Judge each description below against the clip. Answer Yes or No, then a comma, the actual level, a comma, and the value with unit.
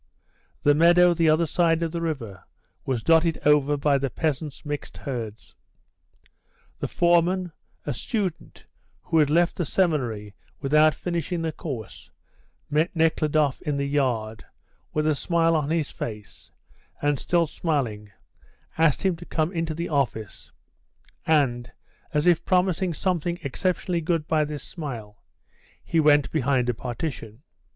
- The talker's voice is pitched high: No, medium, 155 Hz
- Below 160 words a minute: Yes, average, 140 wpm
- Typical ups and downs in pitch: Yes, average, 3.5 semitones